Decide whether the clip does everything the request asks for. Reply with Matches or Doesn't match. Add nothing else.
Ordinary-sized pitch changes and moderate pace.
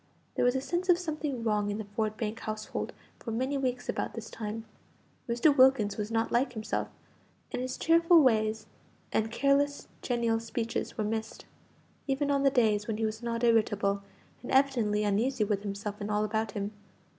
Matches